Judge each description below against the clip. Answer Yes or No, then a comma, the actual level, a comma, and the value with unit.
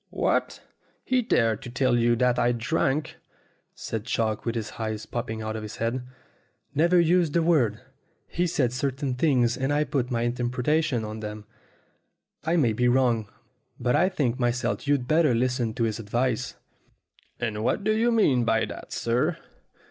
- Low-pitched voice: Yes, low, 125 Hz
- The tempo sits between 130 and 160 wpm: No, average, 170 wpm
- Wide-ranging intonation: No, average, 4.1 semitones